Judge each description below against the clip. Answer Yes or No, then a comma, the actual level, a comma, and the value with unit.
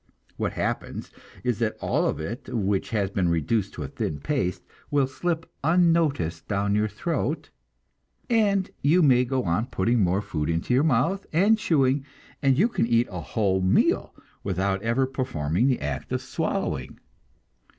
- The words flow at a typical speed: Yes, average, 160 wpm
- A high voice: No, low, 115 Hz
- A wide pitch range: Yes, wide, 7.2 semitones